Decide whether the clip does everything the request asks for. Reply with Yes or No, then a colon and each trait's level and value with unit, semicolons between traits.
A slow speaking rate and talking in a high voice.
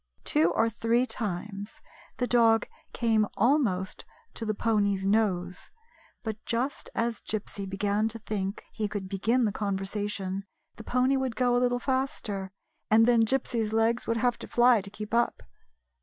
No: average, 155 wpm; high, 220 Hz